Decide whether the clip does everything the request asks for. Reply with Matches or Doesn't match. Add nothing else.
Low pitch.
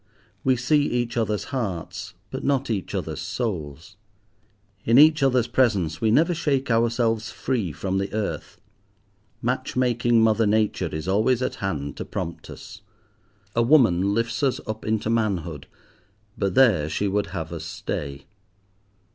Matches